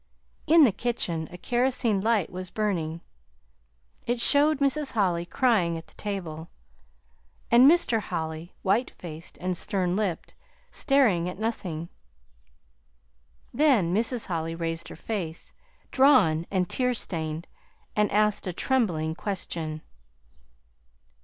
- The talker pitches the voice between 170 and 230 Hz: Yes, high, 190 Hz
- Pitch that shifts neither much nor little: No, wide, 6.0 semitones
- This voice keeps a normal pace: No, slow, 120 wpm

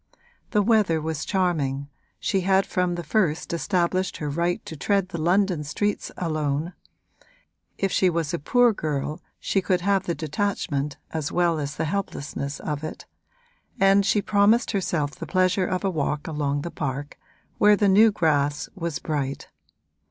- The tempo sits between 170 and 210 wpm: No, average, 160 wpm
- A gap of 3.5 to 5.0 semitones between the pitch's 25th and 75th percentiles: Yes, average, 4.5 semitones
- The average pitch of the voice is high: No, medium, 170 Hz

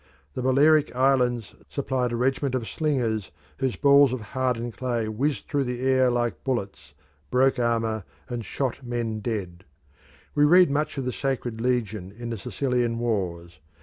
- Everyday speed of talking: Yes, average, 155 wpm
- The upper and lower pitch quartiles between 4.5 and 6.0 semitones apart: No, average, 2.8 semitones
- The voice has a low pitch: Yes, low, 125 Hz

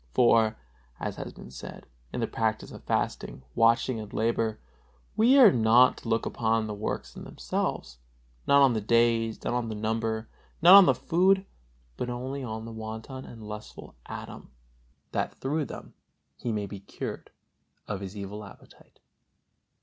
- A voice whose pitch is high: No, low, 115 Hz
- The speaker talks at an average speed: Yes, average, 165 wpm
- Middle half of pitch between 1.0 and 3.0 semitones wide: Yes, narrow, 2.6 semitones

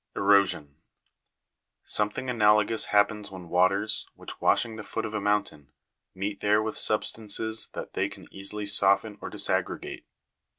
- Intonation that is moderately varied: No, narrow, 1.6 semitones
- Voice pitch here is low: Yes, low, 105 Hz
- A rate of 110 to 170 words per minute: Yes, slow, 135 wpm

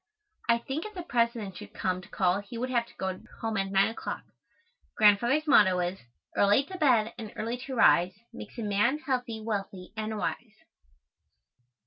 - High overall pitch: Yes, high, 220 Hz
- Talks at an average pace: Yes, average, 175 wpm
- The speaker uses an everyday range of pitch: Yes, average, 3.8 semitones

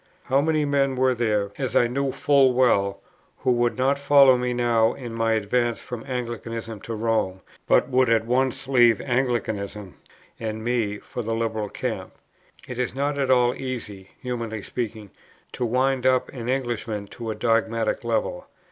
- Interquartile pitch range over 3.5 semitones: No, narrow, 2.6 semitones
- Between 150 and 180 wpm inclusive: Yes, average, 165 wpm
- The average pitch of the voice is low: Yes, low, 120 Hz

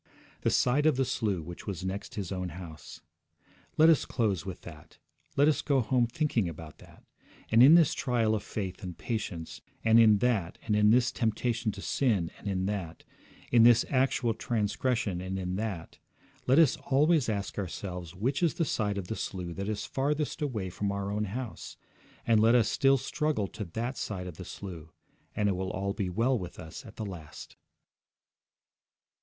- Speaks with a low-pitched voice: Yes, low, 105 Hz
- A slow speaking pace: No, average, 185 wpm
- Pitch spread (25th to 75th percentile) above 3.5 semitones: Yes, average, 4.9 semitones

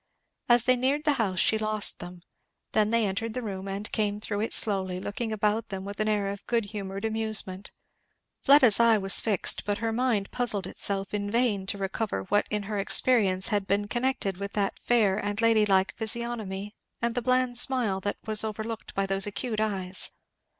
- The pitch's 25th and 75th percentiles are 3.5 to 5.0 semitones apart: No, narrow, 2.6 semitones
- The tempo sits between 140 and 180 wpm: No, average, 190 wpm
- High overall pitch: Yes, high, 210 Hz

